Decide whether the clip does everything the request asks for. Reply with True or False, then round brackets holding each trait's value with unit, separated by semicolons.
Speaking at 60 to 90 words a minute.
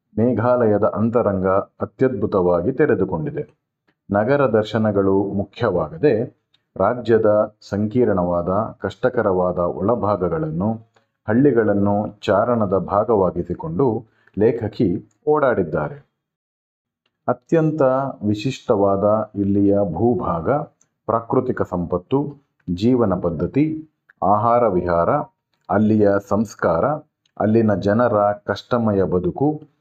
True (65 wpm)